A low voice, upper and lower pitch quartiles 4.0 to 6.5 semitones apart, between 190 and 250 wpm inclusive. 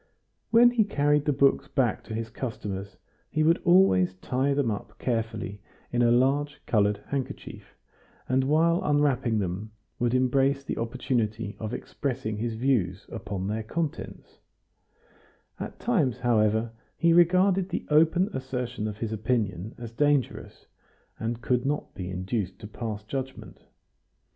No: low, 120 Hz; average, 4.9 semitones; average, 140 wpm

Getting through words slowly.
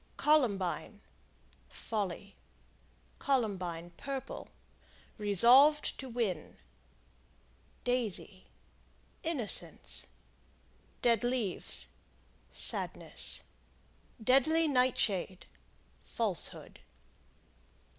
Yes: slow, 50 wpm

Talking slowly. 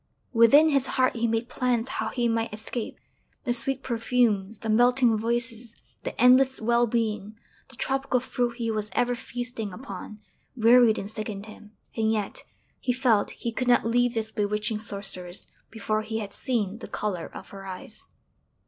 No: average, 165 wpm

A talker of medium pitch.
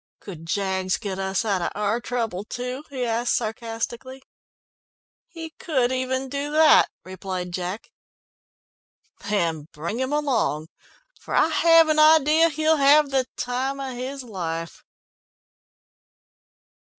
No: high, 245 Hz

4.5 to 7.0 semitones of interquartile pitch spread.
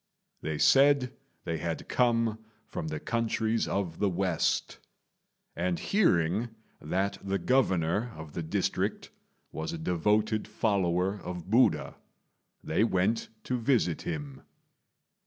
Yes: wide, 5.4 semitones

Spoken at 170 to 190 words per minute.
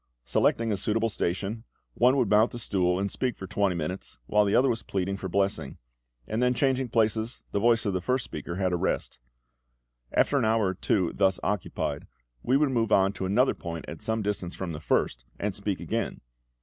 No: fast, 205 wpm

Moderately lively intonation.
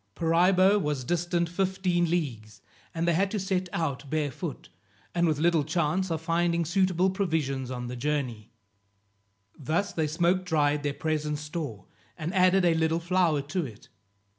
Yes: average, 3.4 semitones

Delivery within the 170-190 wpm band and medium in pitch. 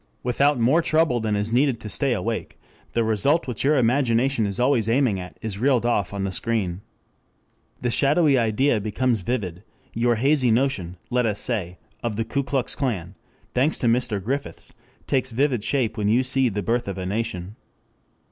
No: average, 180 wpm; low, 120 Hz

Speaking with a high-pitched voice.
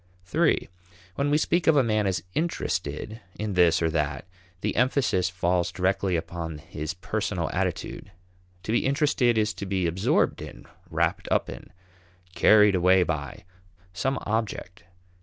No: very low, 95 Hz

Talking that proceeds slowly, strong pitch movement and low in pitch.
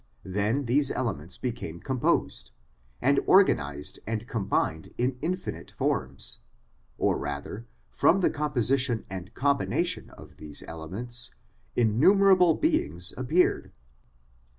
Yes: slow, 105 wpm; wide, 7.8 semitones; low, 120 Hz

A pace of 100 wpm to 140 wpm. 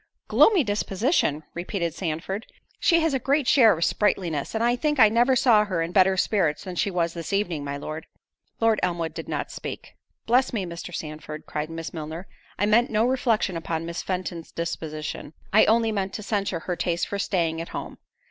No: average, 190 wpm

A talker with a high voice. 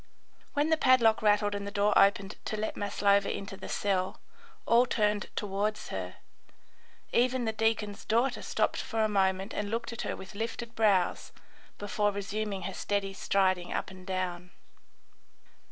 Yes: high, 205 Hz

